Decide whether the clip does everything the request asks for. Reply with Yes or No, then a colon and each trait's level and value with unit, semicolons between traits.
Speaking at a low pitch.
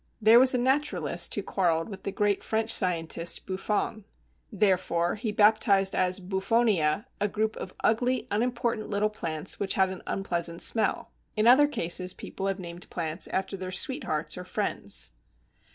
No: high, 195 Hz